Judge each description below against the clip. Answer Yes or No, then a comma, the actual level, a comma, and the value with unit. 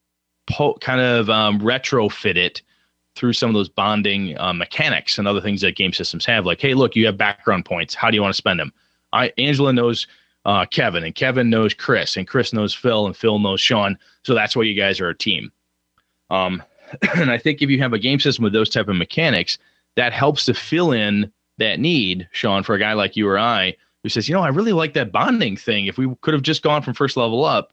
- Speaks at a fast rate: Yes, fast, 235 wpm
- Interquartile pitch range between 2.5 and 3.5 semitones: No, average, 4.3 semitones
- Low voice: Yes, low, 110 Hz